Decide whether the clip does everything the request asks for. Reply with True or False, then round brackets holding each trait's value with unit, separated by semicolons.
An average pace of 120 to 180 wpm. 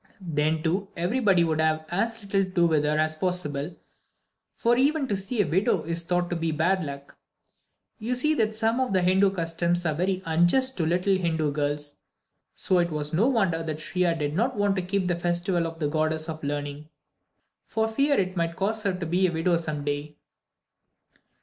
False (200 wpm)